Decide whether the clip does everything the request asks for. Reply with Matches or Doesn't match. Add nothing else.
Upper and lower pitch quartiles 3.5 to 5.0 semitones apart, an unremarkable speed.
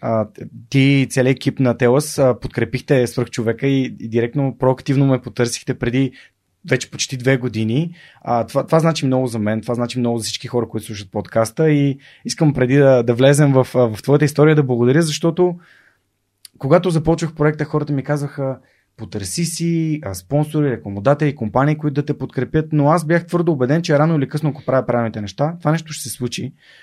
Doesn't match